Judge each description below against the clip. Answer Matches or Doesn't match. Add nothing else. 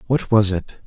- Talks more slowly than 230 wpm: Matches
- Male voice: Matches